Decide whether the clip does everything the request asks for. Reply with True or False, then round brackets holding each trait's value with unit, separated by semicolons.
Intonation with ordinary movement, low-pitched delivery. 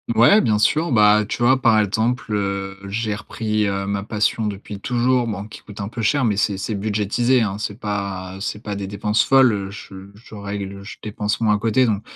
False (2.2 semitones; 105 Hz)